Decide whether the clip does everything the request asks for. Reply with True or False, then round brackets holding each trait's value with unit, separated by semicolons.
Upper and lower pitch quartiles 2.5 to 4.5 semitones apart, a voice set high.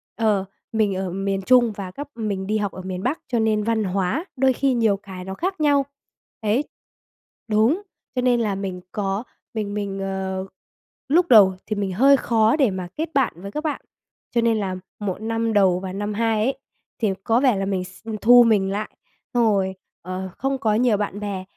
True (3.7 semitones; 210 Hz)